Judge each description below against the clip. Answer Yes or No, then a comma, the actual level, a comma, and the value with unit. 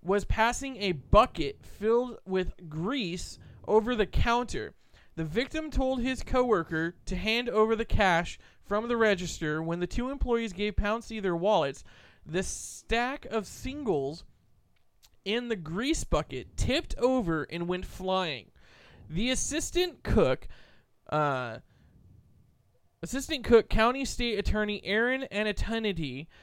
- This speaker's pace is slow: Yes, slow, 125 wpm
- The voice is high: Yes, high, 215 Hz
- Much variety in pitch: No, average, 5.0 semitones